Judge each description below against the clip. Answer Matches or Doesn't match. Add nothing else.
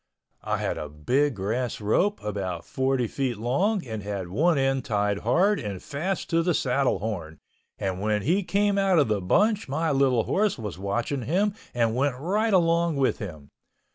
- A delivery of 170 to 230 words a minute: Matches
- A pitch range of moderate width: Doesn't match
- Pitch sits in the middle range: Doesn't match